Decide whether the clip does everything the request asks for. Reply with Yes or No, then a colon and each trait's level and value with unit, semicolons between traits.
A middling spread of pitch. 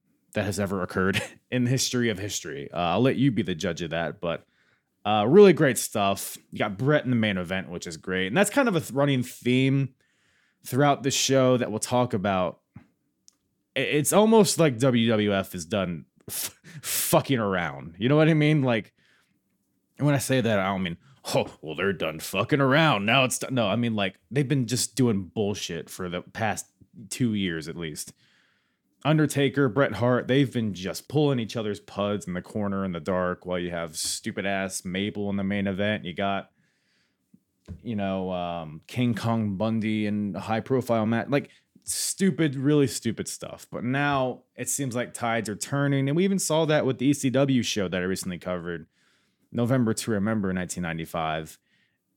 No: wide, 5.9 semitones